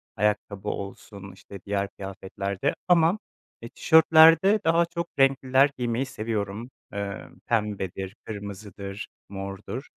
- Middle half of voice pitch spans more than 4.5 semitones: Yes, wide, 5.5 semitones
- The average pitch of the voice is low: Yes, low, 105 Hz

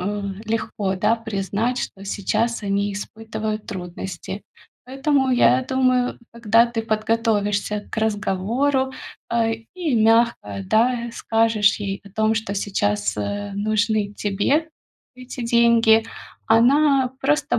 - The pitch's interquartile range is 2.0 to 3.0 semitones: Yes, average, 2.7 semitones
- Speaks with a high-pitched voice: Yes, high, 220 Hz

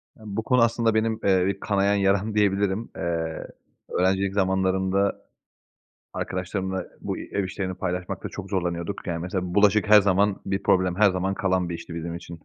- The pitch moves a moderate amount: No, narrow, 1.8 semitones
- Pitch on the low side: Yes, very low, 95 Hz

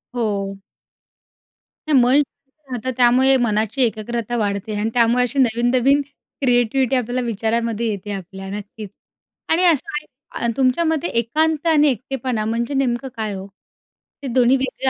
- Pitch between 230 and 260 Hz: Yes, high, 240 Hz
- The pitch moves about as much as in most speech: Yes, average, 3.5 semitones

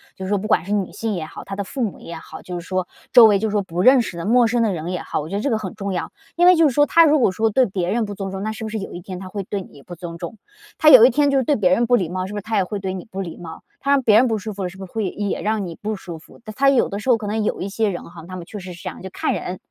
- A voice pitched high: Yes, high, 205 Hz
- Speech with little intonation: No, average, 3.4 semitones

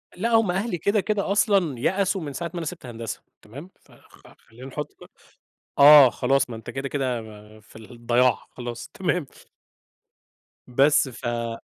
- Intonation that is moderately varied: No, wide, 6.8 semitones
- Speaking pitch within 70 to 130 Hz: No, medium, 140 Hz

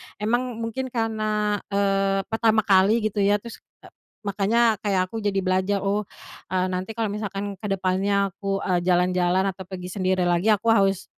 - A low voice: No, high, 200 Hz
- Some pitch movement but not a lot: No, narrow, 2.3 semitones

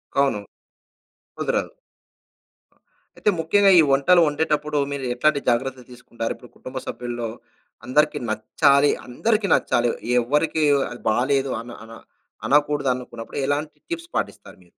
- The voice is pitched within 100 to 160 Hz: Yes, medium, 140 Hz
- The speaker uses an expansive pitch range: No, average, 3.7 semitones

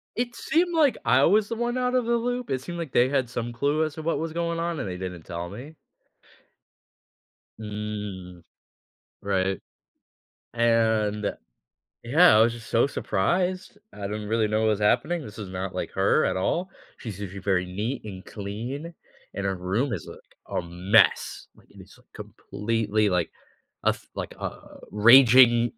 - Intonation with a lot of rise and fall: Yes, wide, 7.8 semitones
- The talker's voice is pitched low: Yes, low, 115 Hz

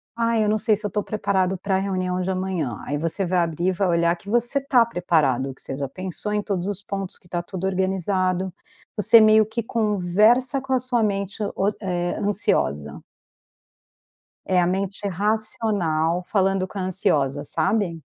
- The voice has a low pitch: No, high, 190 Hz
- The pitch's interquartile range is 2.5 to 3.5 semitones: Yes, average, 3.2 semitones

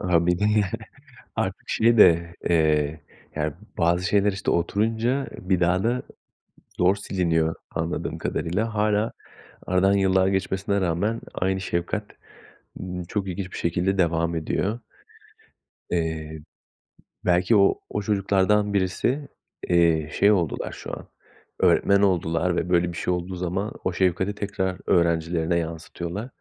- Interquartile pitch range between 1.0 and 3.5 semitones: Yes, average, 3.0 semitones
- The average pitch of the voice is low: Yes, very low, 90 Hz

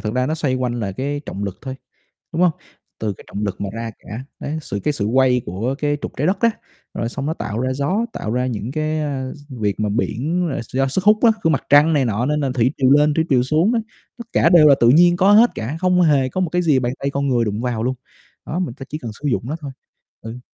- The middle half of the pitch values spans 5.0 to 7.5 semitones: No, average, 4.6 semitones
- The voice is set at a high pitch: No, low, 135 Hz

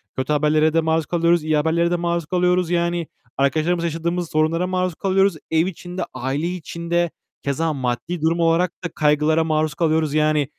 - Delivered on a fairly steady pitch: Yes, narrow, 2.0 semitones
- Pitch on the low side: No, medium, 165 Hz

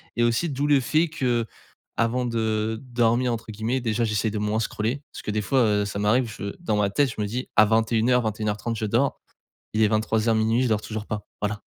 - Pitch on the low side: Yes, low, 110 Hz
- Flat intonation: Yes, narrow, 2.3 semitones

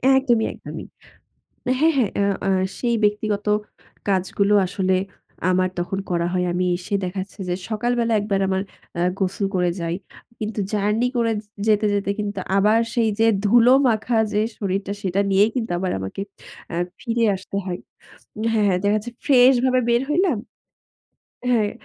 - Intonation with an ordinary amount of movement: Yes, average, 3.4 semitones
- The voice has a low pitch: No, high, 205 Hz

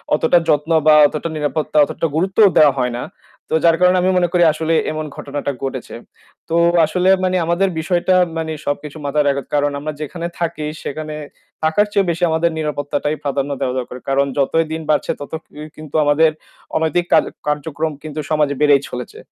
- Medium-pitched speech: Yes, medium, 155 Hz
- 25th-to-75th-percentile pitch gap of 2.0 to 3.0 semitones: Yes, narrow, 2.5 semitones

